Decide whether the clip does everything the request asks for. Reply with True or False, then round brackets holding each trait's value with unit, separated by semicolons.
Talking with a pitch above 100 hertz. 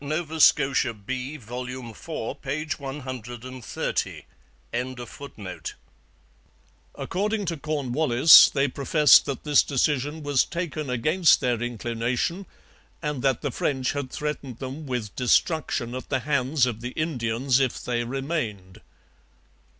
True (135 Hz)